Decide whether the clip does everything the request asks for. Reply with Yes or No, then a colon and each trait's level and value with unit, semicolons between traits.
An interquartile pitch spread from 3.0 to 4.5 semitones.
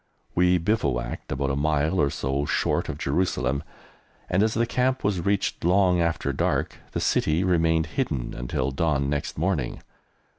No: average, 5.0 semitones